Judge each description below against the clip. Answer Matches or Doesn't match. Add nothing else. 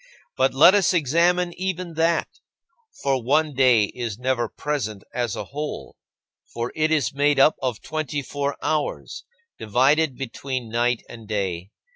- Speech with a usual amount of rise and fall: Matches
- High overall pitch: Doesn't match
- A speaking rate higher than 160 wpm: Doesn't match